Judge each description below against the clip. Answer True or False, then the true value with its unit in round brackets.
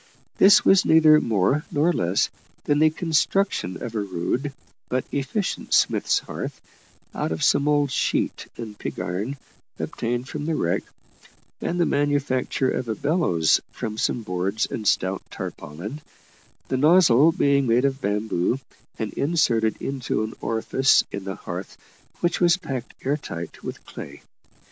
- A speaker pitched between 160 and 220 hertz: False (130 Hz)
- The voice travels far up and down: True (6.0 semitones)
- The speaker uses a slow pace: False (150 wpm)